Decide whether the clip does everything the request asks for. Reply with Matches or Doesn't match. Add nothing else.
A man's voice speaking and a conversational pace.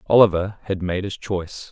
Matches